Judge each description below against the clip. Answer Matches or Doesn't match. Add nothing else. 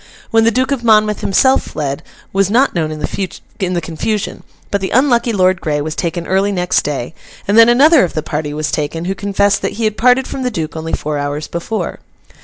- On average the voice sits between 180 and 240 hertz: Matches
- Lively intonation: Matches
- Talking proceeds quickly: Matches